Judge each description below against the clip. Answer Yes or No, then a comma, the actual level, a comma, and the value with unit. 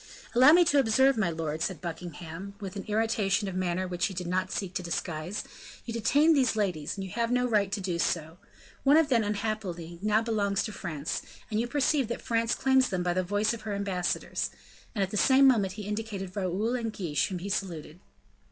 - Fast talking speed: Yes, fast, 215 wpm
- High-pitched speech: Yes, high, 200 Hz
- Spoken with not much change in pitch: No, average, 4.1 semitones